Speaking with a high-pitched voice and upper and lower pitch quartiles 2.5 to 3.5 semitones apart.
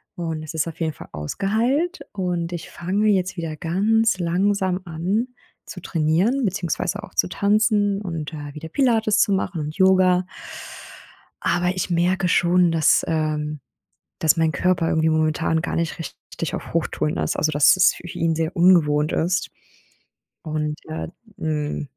No: medium, 170 Hz; average, 3.2 semitones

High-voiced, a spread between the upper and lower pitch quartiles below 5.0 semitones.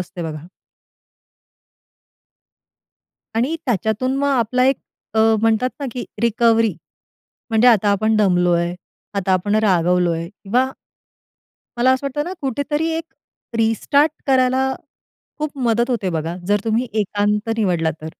No: high, 220 Hz; wide, 5.5 semitones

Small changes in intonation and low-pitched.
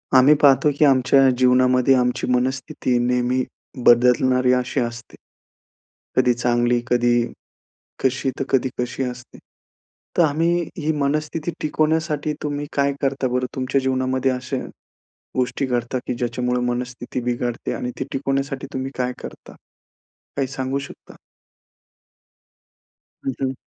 Yes: narrow, 1.8 semitones; low, 130 Hz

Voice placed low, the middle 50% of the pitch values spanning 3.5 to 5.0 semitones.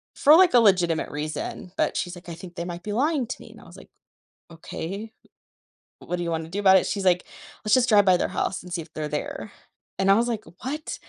No: medium, 185 Hz; average, 4.2 semitones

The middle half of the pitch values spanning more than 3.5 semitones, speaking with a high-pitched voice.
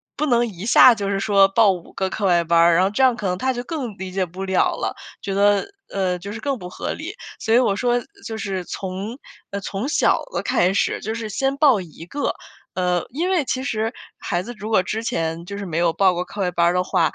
Yes: average, 4.2 semitones; high, 200 Hz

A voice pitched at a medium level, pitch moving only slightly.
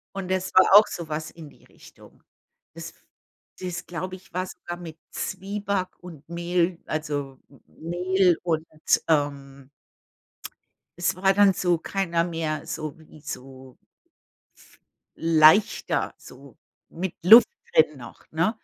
No: medium, 170 Hz; average, 3.1 semitones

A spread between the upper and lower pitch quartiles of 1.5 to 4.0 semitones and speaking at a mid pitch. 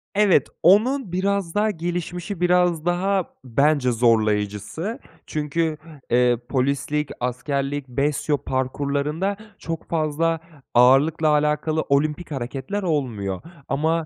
No: average, 4.8 semitones; medium, 150 Hz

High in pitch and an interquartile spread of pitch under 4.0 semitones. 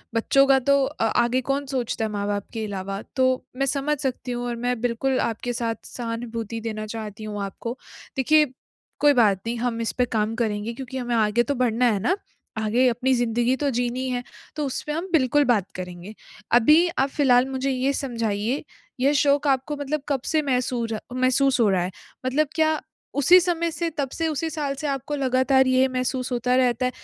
Yes: very high, 255 Hz; average, 3.2 semitones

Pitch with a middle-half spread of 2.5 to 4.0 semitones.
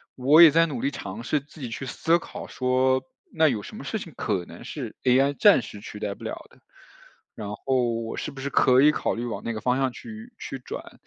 No: average, 4.4 semitones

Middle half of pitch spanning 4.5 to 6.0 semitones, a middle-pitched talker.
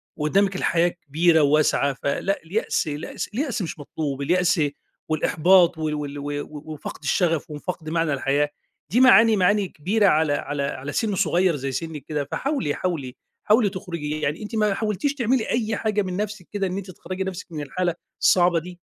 Yes: average, 4.9 semitones; medium, 175 Hz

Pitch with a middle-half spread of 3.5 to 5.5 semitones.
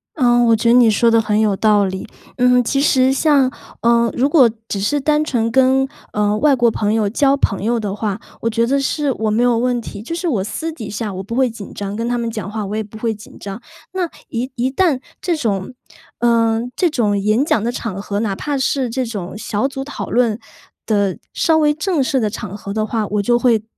Yes: average, 3.9 semitones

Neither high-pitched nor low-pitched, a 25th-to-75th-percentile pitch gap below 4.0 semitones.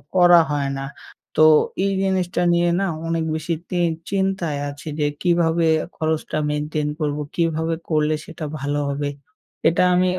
Yes: medium, 160 Hz; average, 2.9 semitones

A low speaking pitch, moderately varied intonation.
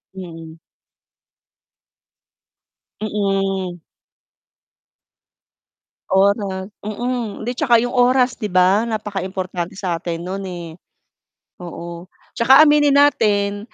No: high, 200 Hz; average, 4.2 semitones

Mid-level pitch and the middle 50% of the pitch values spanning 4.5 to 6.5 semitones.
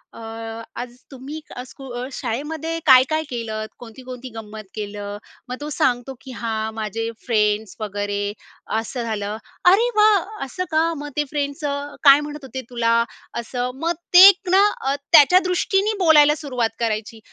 No: very high, 255 Hz; average, 5.0 semitones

